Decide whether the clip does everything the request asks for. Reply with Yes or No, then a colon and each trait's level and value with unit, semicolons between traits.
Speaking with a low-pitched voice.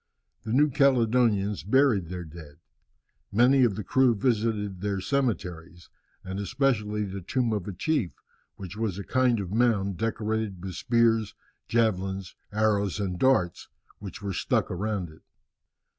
Yes: low, 105 Hz